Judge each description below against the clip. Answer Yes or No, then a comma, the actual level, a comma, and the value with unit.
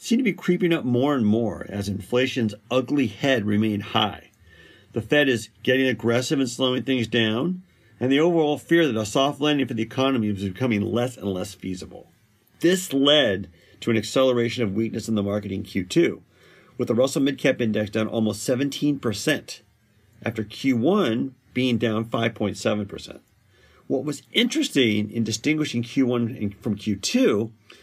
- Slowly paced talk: No, average, 160 wpm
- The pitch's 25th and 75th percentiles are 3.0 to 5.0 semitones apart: Yes, average, 4.1 semitones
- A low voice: Yes, low, 115 Hz